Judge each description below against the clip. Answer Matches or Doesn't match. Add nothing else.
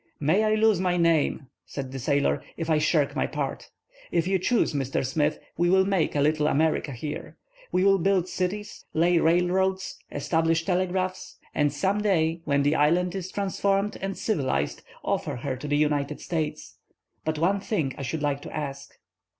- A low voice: Doesn't match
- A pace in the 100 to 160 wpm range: Doesn't match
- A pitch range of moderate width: Matches